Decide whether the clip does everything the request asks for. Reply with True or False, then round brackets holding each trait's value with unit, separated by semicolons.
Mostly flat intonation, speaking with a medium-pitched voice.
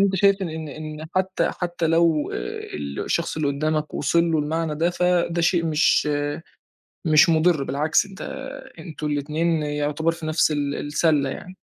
True (2.3 semitones; 160 Hz)